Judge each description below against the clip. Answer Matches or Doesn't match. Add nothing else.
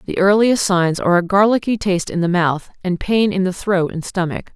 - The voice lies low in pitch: Doesn't match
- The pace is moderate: Doesn't match